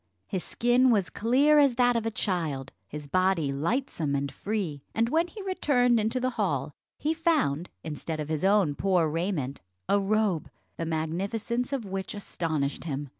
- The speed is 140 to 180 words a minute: Yes, average, 170 wpm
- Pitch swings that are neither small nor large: No, wide, 7.6 semitones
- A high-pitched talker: Yes, high, 195 Hz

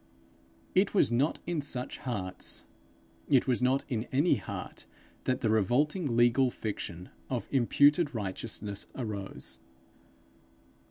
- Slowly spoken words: Yes, slow, 115 wpm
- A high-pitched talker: No, low, 125 Hz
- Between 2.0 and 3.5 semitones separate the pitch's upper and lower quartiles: No, average, 4.4 semitones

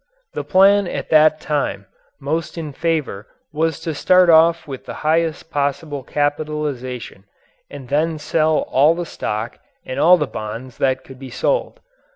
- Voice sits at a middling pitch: Yes, medium, 150 Hz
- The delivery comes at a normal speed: Yes, average, 155 wpm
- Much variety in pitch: No, average, 3.5 semitones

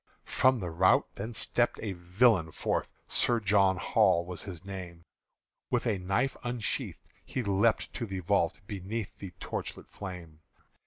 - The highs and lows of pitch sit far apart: No, average, 3.8 semitones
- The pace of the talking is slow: No, average, 150 wpm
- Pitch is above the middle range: No, very low, 95 Hz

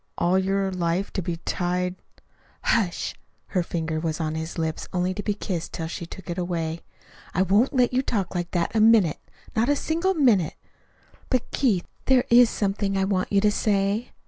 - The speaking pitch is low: No, high, 190 Hz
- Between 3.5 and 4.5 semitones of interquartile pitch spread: Yes, average, 3.9 semitones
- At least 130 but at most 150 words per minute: No, average, 195 wpm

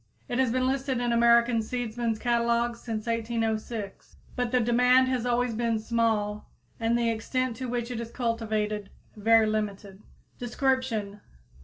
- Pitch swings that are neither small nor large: No, narrow, 1.8 semitones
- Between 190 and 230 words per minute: No, average, 145 wpm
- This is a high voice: Yes, high, 235 Hz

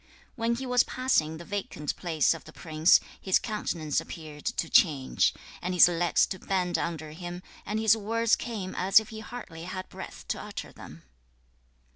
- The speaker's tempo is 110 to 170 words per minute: No, average, 180 wpm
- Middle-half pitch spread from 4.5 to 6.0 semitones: Yes, average, 5.1 semitones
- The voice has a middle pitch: Yes, medium, 180 Hz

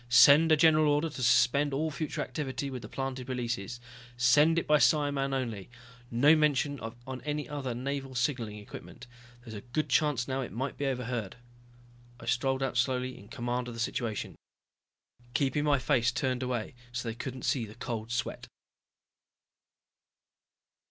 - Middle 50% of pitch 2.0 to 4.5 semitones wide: Yes, average, 3.0 semitones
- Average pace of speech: Yes, average, 160 wpm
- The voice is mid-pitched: No, low, 130 Hz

